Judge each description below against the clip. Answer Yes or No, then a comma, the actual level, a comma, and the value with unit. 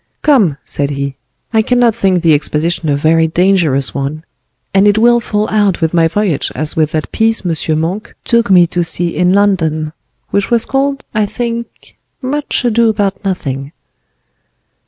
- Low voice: No, medium, 185 Hz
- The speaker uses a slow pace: No, average, 165 wpm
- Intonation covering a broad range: Yes, wide, 5.8 semitones